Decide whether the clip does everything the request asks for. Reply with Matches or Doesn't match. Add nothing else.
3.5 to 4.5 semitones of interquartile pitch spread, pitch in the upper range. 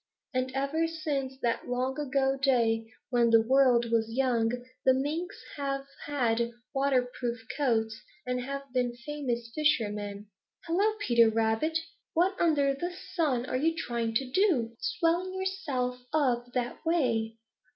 Matches